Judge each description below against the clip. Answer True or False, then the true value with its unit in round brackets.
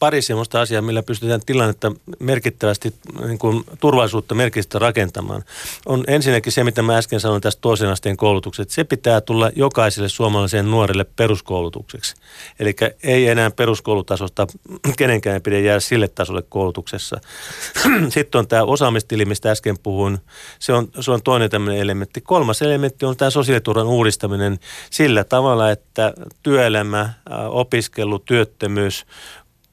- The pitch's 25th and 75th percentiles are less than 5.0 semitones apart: True (3.1 semitones)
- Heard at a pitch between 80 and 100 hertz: False (115 Hz)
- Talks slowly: False (135 wpm)